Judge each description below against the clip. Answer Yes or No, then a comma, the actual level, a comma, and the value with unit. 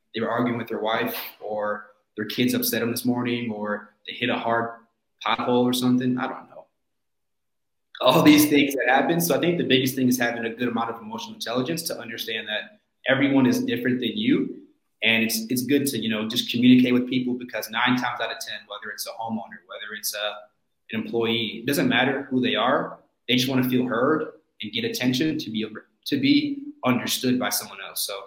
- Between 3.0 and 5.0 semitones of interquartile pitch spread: No, narrow, 2.4 semitones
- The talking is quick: Yes, fast, 215 wpm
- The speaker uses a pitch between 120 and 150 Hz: Yes, low, 125 Hz